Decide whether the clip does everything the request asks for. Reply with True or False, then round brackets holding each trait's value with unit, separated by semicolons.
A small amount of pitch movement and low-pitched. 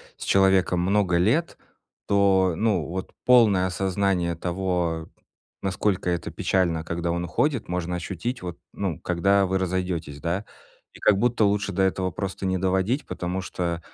True (2.1 semitones; 95 Hz)